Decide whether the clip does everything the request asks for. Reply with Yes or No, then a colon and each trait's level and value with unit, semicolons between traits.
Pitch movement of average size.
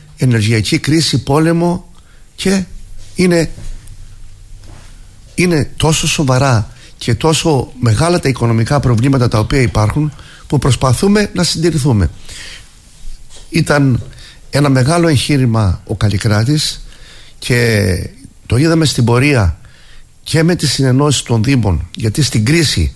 No: wide, 5.9 semitones